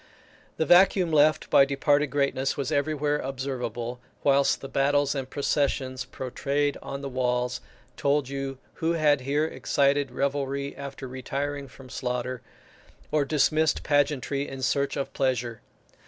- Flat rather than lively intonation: Yes, narrow, 1.6 semitones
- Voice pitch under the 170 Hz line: Yes, medium, 140 Hz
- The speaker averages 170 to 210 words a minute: No, slow, 135 wpm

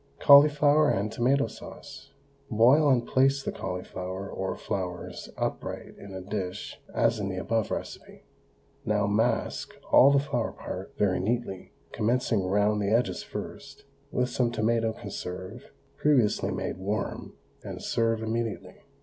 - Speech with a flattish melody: No, average, 4.2 semitones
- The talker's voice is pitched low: Yes, low, 110 Hz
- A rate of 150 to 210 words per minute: No, slow, 135 wpm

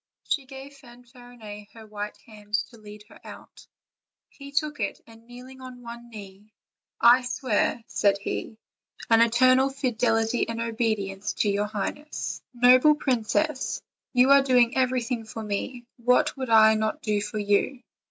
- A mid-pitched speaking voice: No, high, 235 Hz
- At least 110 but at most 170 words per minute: Yes, average, 150 wpm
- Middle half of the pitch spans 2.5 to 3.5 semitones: Yes, average, 3.1 semitones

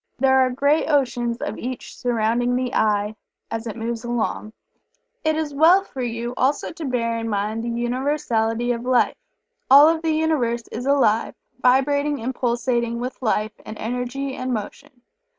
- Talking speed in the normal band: Yes, average, 165 wpm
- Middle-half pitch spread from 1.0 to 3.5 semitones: Yes, average, 2.8 semitones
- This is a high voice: Yes, high, 245 Hz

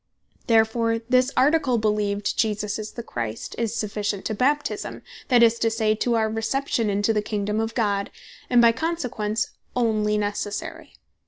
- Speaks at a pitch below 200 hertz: No, high, 220 Hz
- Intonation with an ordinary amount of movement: No, narrow, 2.1 semitones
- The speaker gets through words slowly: No, average, 155 wpm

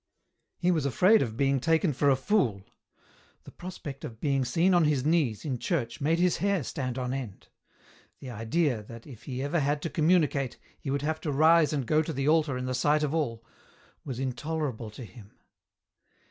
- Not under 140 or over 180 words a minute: No, average, 195 wpm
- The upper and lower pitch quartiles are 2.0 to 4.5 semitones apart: Yes, average, 4.2 semitones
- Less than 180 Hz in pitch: Yes, medium, 140 Hz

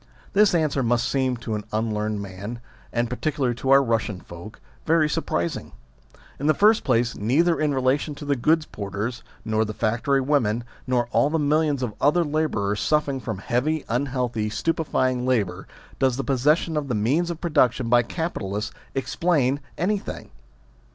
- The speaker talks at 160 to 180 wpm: Yes, average, 165 wpm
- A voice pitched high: No, low, 130 Hz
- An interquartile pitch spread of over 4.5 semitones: Yes, average, 5.1 semitones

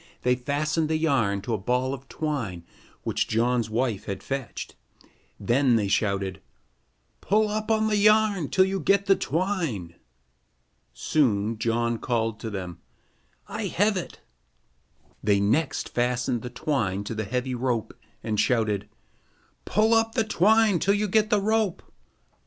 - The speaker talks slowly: No, average, 145 wpm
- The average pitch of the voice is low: Yes, low, 130 Hz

